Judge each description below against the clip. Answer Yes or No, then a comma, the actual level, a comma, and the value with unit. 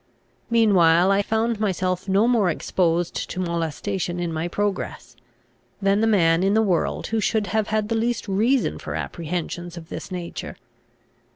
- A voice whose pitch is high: Yes, high, 195 Hz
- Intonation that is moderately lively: Yes, average, 3.9 semitones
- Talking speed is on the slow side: No, average, 160 wpm